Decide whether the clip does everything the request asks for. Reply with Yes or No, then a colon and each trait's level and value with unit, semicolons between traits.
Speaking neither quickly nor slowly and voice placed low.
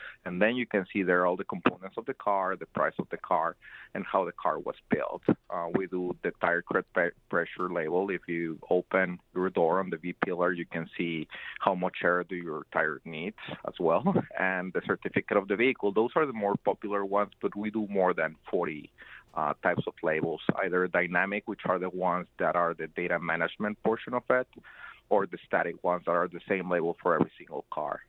No: fast, 215 wpm; very low, 90 Hz